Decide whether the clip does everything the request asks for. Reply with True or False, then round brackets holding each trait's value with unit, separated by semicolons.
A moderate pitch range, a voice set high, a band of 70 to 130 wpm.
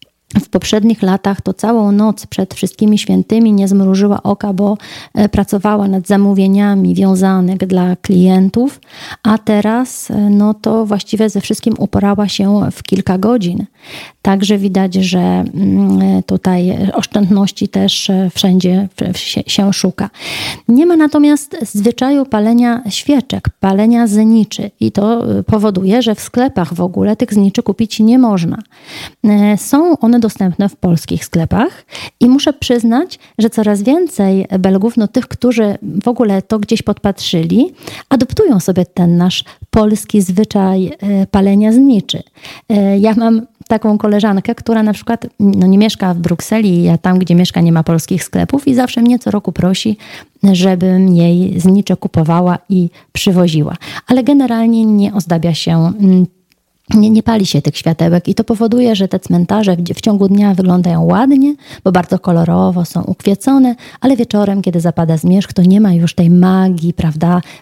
False (3.2 semitones; 200 Hz; 145 wpm)